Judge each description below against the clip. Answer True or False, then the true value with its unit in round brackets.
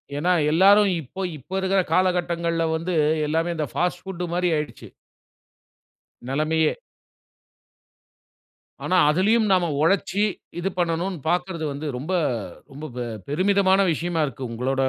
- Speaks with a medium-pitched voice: True (175 Hz)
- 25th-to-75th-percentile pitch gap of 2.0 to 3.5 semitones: True (3.2 semitones)